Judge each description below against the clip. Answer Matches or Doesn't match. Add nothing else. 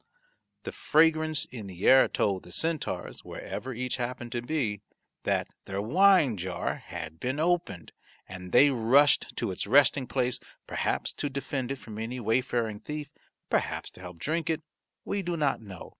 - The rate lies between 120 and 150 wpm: Doesn't match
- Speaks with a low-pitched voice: Matches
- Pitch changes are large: Matches